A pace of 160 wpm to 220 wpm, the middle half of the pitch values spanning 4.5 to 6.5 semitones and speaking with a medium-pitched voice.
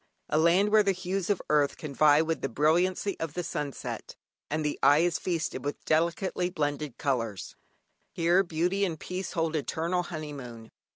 No: average, 170 wpm; average, 3.4 semitones; medium, 160 Hz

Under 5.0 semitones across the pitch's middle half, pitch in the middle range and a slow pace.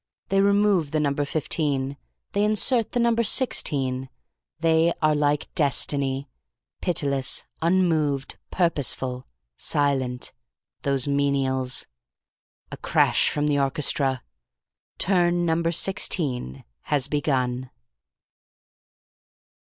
Yes: average, 4.0 semitones; medium, 145 Hz; slow, 90 wpm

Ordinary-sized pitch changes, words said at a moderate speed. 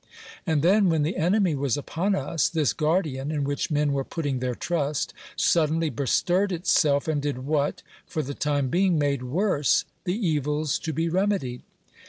Yes: average, 3.3 semitones; average, 170 wpm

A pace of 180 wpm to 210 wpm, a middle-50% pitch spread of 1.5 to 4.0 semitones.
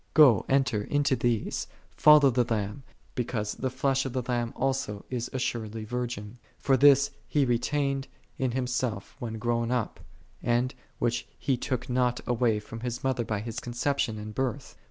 No: average, 160 wpm; average, 2.7 semitones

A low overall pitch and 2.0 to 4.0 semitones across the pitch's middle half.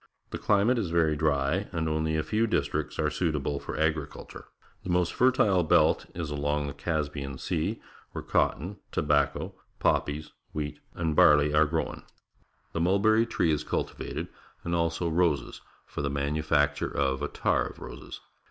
Yes: very low, 80 Hz; average, 2.9 semitones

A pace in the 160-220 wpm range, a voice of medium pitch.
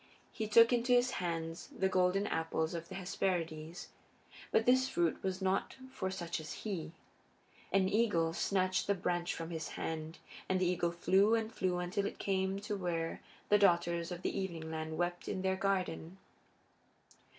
Yes: average, 170 wpm; medium, 180 Hz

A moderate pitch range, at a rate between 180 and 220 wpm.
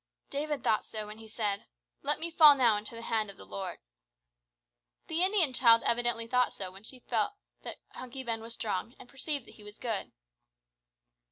Yes: average, 3.8 semitones; average, 190 wpm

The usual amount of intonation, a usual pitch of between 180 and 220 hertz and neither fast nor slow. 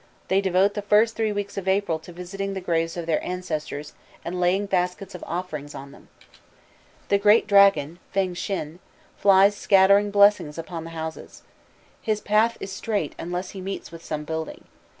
Yes: average, 3.3 semitones; high, 190 Hz; average, 170 wpm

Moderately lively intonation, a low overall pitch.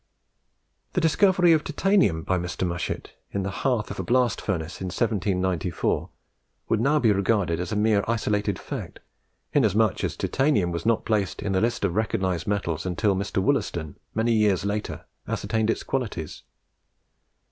Yes: average, 3.9 semitones; low, 105 Hz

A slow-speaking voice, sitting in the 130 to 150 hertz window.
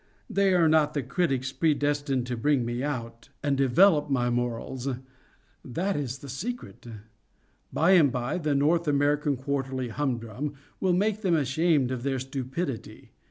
No: average, 145 wpm; medium, 140 Hz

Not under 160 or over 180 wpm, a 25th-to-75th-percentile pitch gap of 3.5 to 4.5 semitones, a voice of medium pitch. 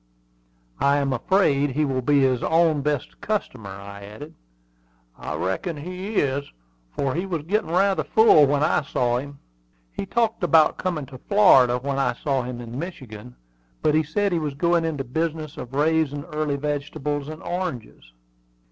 Yes: average, 170 wpm; average, 4.0 semitones; medium, 145 Hz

